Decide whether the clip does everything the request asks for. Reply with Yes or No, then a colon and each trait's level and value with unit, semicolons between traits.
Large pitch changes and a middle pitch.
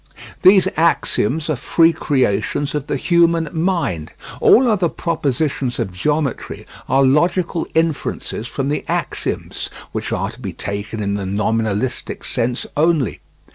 Yes: wide, 6.6 semitones; medium, 145 Hz